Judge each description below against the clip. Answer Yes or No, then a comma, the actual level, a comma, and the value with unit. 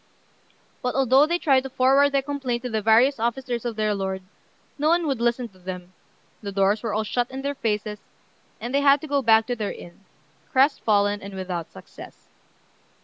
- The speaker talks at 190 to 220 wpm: Yes, average, 195 wpm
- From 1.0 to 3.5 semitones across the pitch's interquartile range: No, average, 4.5 semitones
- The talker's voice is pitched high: Yes, high, 235 Hz